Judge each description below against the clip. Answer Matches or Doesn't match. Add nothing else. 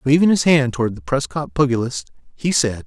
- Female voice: Doesn't match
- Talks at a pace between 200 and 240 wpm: Doesn't match